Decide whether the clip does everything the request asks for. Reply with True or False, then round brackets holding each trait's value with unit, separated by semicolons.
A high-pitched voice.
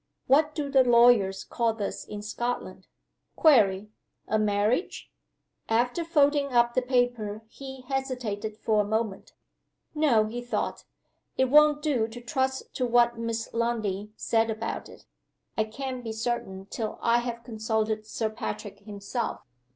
True (235 Hz)